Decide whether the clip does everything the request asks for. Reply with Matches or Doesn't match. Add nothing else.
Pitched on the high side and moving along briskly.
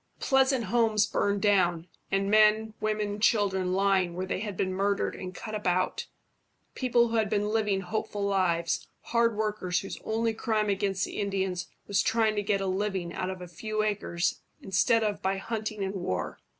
Doesn't match